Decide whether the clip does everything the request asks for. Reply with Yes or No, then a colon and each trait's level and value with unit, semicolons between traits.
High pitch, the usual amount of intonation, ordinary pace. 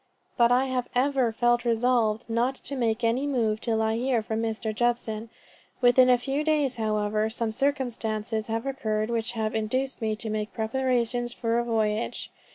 No: high, 235 Hz; narrow, 2.3 semitones; average, 170 wpm